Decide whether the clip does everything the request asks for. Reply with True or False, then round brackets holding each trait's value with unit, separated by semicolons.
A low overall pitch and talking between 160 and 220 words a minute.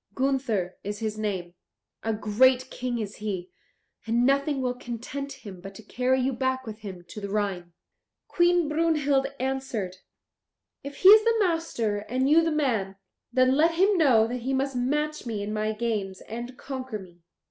False (250 Hz; 175 wpm)